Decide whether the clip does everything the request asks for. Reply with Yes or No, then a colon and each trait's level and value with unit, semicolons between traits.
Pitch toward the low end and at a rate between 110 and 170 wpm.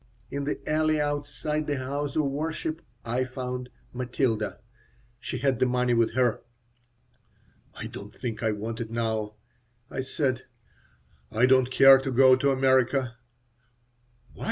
Yes: low, 130 Hz; average, 140 wpm